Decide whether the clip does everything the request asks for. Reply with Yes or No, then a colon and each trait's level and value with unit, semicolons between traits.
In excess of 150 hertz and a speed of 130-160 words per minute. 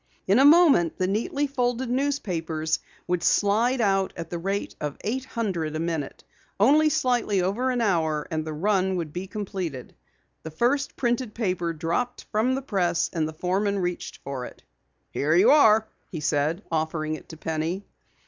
No: high, 190 Hz; average, 170 wpm